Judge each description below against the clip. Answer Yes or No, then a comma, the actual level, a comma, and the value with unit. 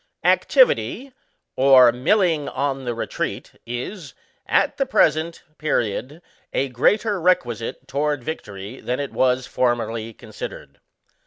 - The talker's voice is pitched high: No, low, 135 Hz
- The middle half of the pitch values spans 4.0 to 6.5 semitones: Yes, average, 5.1 semitones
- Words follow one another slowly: Yes, slow, 110 wpm